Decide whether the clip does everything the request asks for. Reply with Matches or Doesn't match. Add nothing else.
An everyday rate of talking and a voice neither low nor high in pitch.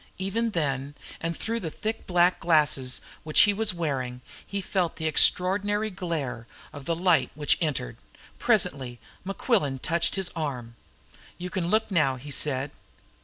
Matches